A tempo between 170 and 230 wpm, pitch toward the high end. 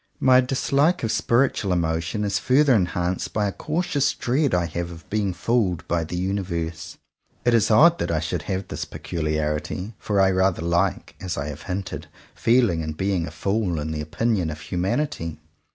No: average, 180 wpm; very low, 95 Hz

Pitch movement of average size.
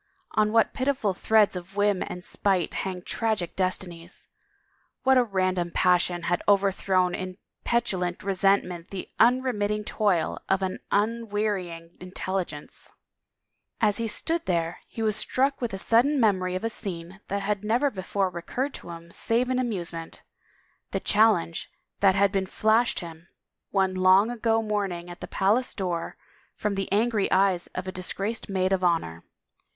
Yes: average, 3.2 semitones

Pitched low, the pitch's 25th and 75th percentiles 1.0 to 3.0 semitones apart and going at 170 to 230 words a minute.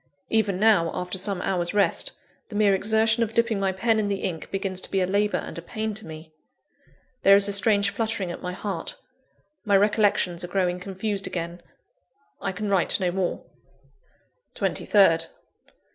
No: high, 195 Hz; average, 2.7 semitones; average, 175 wpm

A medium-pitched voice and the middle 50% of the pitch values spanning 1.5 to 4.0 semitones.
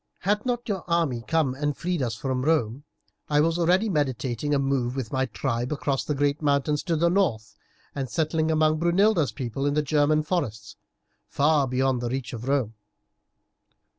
Yes: medium, 145 Hz; average, 3.7 semitones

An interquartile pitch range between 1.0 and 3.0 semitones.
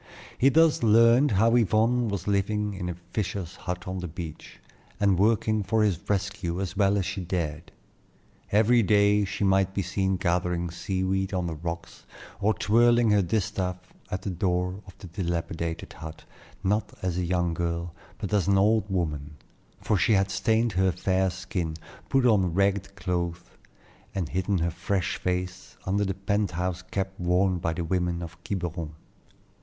Yes: narrow, 2.6 semitones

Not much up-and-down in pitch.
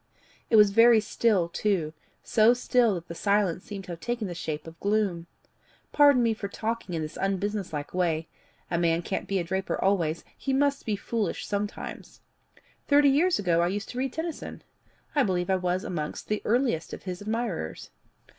No: average, 5.0 semitones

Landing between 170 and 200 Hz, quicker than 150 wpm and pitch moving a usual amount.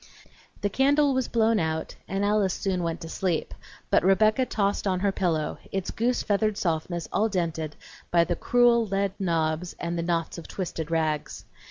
Yes: medium, 185 Hz; average, 175 wpm; average, 4.2 semitones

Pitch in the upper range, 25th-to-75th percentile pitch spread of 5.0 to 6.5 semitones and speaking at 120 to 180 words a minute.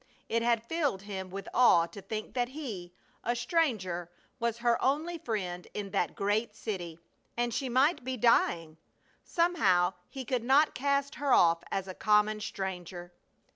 Yes: high, 220 Hz; wide, 5.5 semitones; average, 160 wpm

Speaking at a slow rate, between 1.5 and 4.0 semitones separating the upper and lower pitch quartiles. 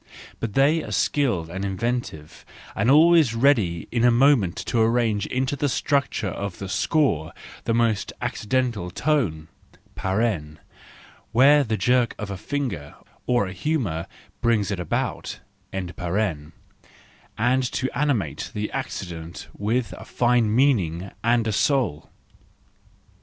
No: slow, 125 wpm; wide, 5.6 semitones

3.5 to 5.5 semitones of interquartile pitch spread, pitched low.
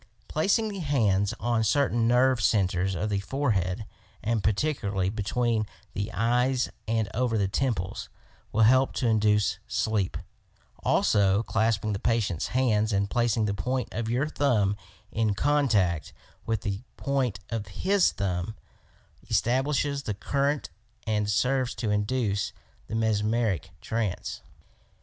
Yes: average, 3.9 semitones; low, 110 Hz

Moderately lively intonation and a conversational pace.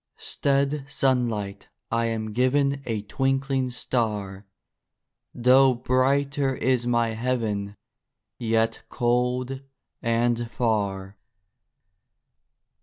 No: average, 3.0 semitones; slow, 80 wpm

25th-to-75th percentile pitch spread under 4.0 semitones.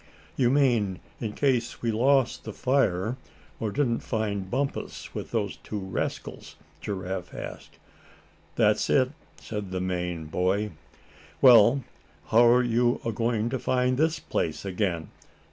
No: average, 4.7 semitones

